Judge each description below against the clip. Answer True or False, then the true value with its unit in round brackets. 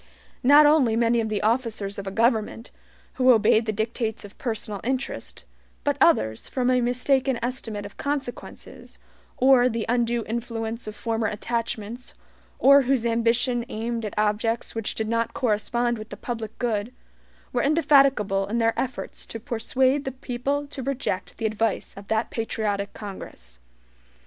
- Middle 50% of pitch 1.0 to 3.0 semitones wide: True (2.6 semitones)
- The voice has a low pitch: False (230 Hz)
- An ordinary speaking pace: True (150 wpm)